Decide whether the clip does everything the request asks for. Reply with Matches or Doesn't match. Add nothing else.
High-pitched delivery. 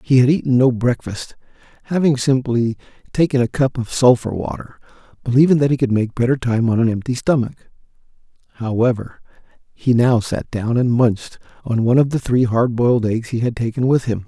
Doesn't match